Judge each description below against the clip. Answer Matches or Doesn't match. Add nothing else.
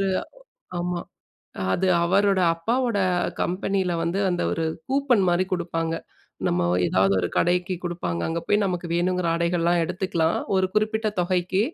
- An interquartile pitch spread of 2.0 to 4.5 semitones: Matches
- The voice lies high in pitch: Doesn't match